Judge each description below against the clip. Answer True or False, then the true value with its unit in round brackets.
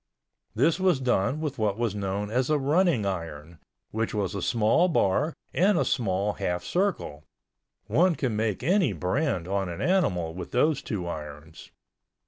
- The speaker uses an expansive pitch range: True (8.7 semitones)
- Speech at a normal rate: True (155 wpm)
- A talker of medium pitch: False (110 Hz)